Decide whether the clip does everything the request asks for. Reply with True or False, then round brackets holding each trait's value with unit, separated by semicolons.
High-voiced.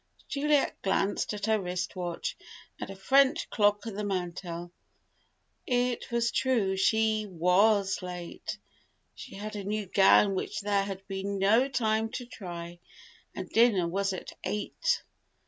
True (200 Hz)